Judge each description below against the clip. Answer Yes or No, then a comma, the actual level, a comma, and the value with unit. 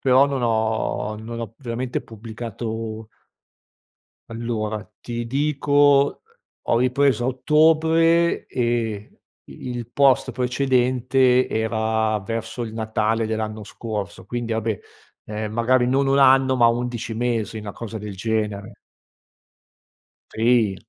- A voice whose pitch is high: No, low, 115 Hz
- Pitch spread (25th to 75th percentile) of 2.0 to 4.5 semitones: Yes, average, 2.8 semitones